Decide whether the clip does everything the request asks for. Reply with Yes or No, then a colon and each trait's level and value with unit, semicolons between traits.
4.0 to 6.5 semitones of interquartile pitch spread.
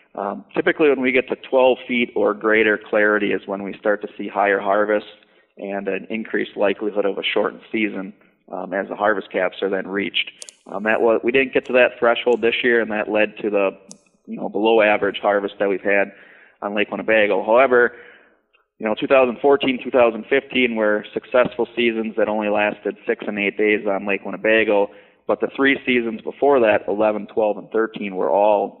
No: average, 2.9 semitones